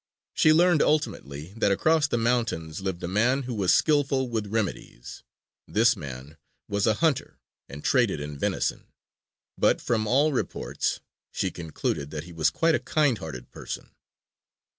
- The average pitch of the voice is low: Yes, low, 110 Hz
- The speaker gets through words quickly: No, average, 155 wpm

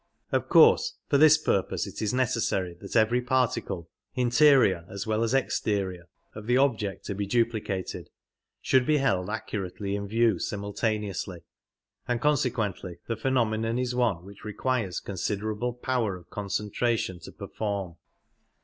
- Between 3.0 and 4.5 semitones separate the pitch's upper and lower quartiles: Yes, average, 3.9 semitones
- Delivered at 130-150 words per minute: Yes, average, 140 wpm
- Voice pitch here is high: No, low, 110 Hz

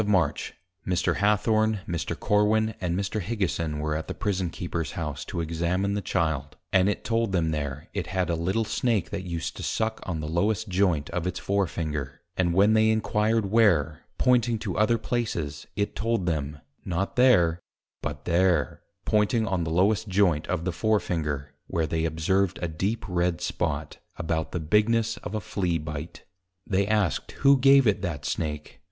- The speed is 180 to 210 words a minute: Yes, average, 185 wpm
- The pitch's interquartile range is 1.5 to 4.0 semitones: No, average, 4.6 semitones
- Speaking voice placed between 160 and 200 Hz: No, very low, 90 Hz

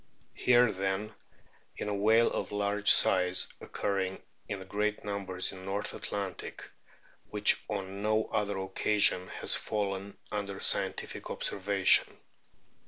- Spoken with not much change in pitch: Yes, narrow, 1.4 semitones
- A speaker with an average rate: No, slow, 120 wpm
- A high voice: No, low, 100 Hz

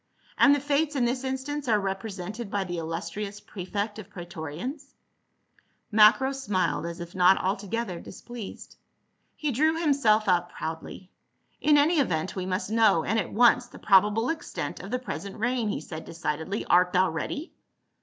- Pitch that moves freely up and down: Yes, wide, 5.7 semitones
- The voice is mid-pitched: No, high, 210 Hz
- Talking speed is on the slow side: No, average, 165 wpm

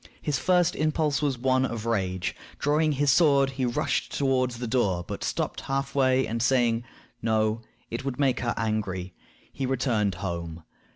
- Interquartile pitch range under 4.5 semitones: Yes, average, 3.9 semitones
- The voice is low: Yes, low, 125 Hz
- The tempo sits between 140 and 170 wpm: Yes, average, 165 wpm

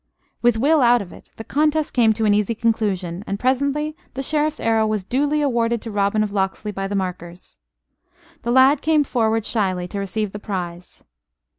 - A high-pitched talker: Yes, high, 220 Hz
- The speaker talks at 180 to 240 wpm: Yes, average, 185 wpm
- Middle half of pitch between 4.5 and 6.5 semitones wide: Yes, average, 4.8 semitones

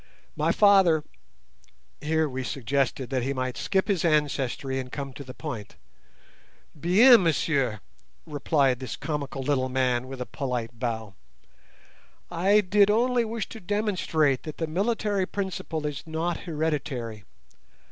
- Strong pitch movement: Yes, wide, 5.9 semitones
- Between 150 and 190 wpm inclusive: No, slow, 135 wpm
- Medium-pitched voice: Yes, medium, 150 Hz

